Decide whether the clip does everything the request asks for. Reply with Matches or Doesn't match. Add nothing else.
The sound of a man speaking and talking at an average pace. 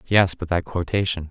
Matches